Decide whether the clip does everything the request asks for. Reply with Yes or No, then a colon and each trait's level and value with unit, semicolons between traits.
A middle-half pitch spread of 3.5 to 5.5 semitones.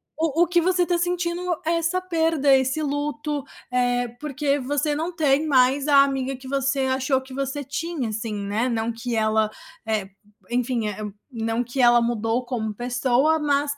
Yes: average, 3.8 semitones